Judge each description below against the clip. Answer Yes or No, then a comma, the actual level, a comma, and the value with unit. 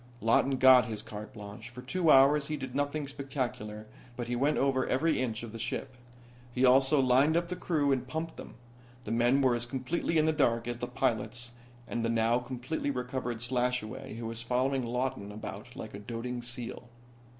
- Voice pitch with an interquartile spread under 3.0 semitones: Yes, narrow, 2.5 semitones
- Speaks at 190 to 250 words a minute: Yes, average, 195 wpm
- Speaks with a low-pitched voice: Yes, low, 125 Hz